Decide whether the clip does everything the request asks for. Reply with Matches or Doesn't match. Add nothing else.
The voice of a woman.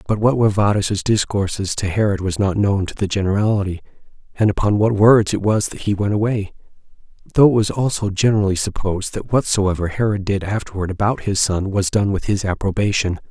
Doesn't match